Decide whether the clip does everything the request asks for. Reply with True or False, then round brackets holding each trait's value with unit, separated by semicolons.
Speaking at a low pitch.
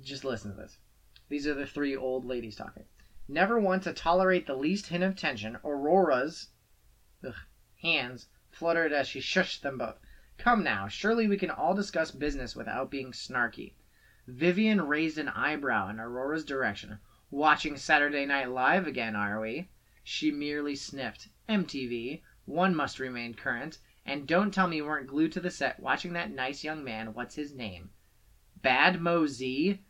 False (145 Hz)